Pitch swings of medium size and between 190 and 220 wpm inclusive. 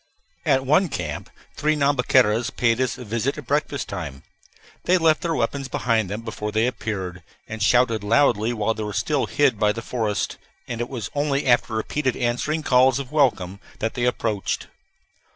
No: average, 4.2 semitones; average, 175 wpm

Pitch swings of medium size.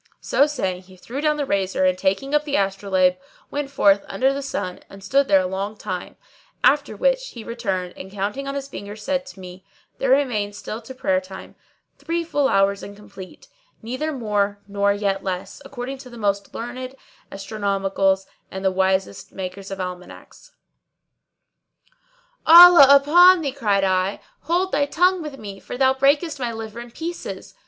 No: wide, 6.2 semitones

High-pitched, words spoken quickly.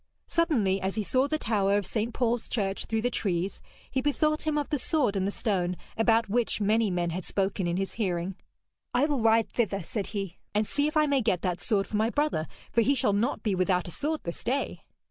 Yes: high, 215 Hz; fast, 230 wpm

